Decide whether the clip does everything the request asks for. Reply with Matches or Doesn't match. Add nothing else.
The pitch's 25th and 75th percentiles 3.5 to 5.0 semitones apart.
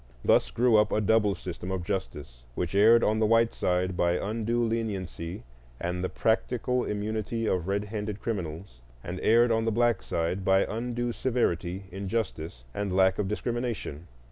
Matches